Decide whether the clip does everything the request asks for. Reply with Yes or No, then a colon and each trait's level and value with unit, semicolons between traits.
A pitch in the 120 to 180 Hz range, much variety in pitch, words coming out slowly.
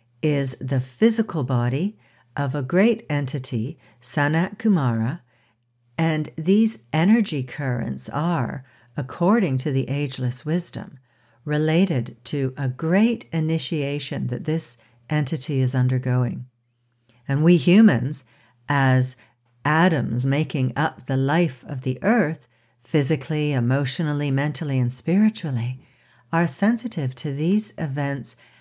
No: medium, 140 Hz; average, 4.4 semitones; slow, 110 wpm